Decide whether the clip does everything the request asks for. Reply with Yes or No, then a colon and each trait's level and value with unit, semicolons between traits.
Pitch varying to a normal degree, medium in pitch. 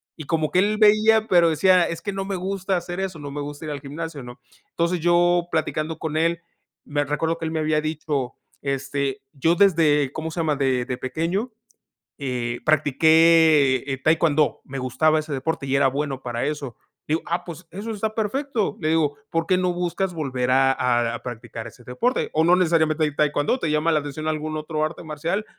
Yes: average, 3.4 semitones; medium, 155 Hz